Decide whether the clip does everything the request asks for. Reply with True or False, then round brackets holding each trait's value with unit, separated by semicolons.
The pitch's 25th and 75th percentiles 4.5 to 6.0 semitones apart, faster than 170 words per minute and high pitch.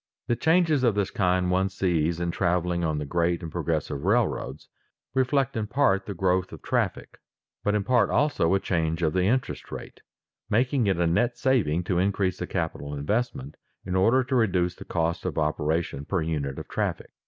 False (5.5 semitones; 190 wpm; 90 Hz)